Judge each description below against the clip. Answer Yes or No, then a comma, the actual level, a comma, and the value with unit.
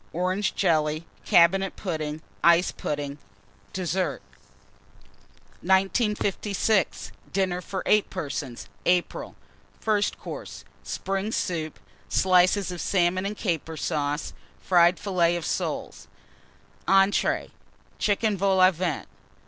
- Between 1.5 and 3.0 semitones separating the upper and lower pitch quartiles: Yes, narrow, 2.6 semitones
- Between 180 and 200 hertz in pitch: Yes, medium, 185 Hz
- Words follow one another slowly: Yes, slow, 95 wpm